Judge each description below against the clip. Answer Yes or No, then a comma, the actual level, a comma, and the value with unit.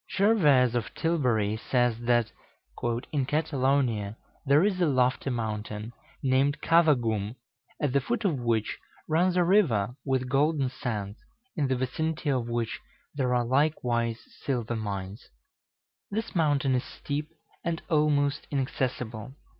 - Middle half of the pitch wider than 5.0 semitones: No, average, 4.3 semitones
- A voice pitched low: Yes, low, 130 Hz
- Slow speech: Yes, slow, 130 wpm